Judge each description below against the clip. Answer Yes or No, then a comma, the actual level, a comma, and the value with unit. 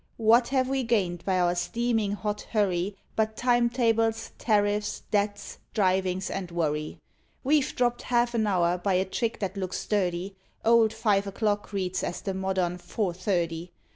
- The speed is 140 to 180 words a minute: Yes, average, 160 wpm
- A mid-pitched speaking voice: No, high, 205 Hz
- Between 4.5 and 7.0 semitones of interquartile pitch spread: No, average, 3.7 semitones